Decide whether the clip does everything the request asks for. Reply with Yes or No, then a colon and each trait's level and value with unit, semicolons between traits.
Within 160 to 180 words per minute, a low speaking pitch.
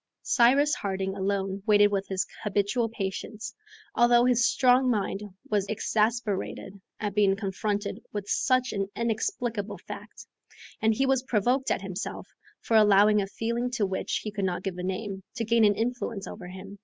No: average, 165 wpm; high, 210 Hz